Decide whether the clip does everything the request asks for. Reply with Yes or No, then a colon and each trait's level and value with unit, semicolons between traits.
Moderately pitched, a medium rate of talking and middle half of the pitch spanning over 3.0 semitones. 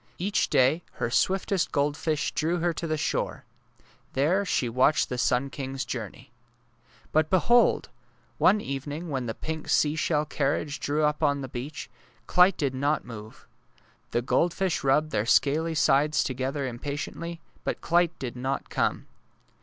Yes: medium, 145 Hz; average, 150 wpm; average, 3.5 semitones